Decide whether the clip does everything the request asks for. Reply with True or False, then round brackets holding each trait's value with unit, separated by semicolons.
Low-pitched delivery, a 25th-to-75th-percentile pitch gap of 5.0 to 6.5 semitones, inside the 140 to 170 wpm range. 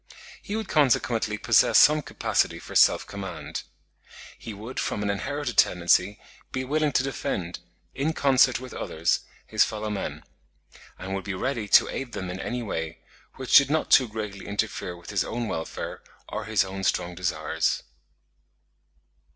True (105 Hz; 5.6 semitones; 160 wpm)